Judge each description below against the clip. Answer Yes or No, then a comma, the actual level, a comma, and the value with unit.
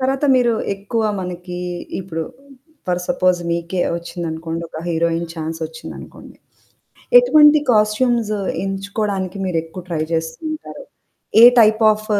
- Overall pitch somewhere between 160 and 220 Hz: Yes, medium, 185 Hz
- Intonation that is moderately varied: Yes, average, 4.5 semitones